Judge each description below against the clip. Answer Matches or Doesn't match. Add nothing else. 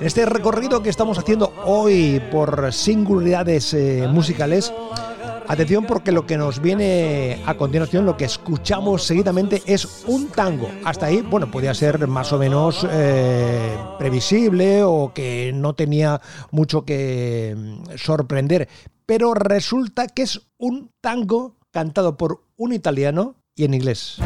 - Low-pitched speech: Doesn't match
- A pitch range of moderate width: Doesn't match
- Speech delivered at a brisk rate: Doesn't match